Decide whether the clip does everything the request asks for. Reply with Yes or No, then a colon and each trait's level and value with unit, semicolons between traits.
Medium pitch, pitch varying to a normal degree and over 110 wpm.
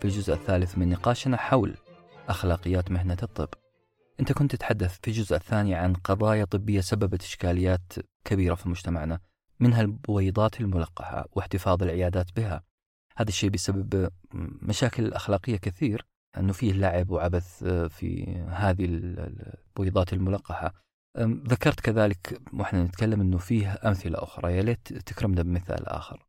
No: very low, 95 Hz; average, 3.5 semitones; average, 130 wpm